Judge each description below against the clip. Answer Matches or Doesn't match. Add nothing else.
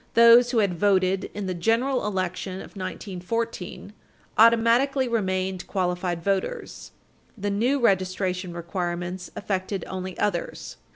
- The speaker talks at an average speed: Doesn't match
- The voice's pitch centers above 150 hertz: Matches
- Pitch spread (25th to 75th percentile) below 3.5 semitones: Doesn't match